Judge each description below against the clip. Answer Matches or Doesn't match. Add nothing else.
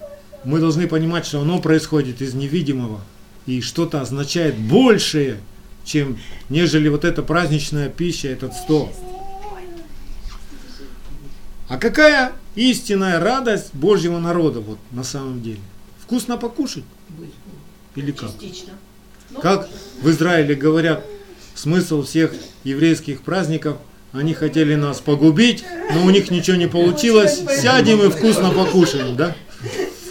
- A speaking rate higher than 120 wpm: Doesn't match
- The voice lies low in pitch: Doesn't match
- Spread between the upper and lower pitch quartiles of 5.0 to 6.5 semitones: Matches